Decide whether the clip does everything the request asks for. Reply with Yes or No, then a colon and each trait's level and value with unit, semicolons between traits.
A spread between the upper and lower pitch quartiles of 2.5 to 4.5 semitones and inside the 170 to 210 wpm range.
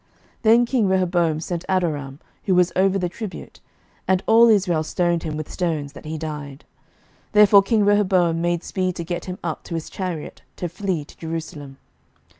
Yes: average, 3.1 semitones; average, 180 wpm